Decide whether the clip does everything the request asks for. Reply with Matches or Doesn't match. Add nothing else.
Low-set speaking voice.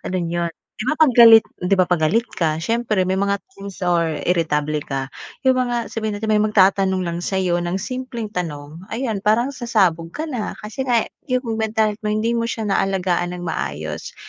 Doesn't match